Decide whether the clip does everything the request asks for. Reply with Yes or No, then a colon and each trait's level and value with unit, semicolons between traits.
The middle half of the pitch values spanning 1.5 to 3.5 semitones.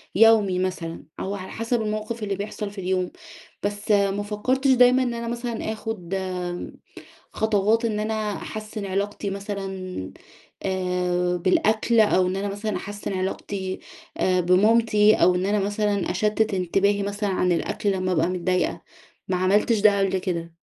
Yes: narrow, 2.5 semitones